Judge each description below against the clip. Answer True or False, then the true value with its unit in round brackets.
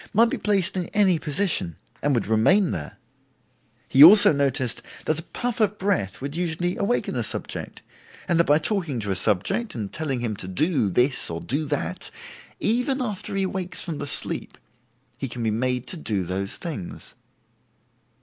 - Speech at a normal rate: True (180 wpm)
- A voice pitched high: False (150 Hz)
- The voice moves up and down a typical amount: False (8.9 semitones)